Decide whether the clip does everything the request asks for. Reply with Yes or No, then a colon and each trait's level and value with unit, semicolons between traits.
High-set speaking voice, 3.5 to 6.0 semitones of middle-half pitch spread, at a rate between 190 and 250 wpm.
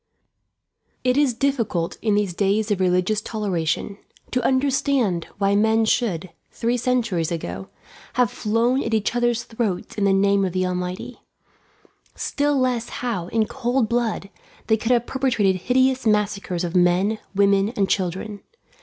No: high, 215 Hz; average, 4.3 semitones; average, 145 wpm